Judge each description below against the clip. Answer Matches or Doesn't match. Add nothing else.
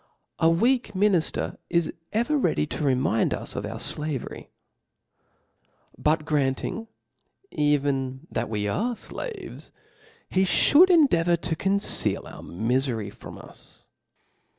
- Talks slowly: Matches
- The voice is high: Doesn't match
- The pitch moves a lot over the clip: Matches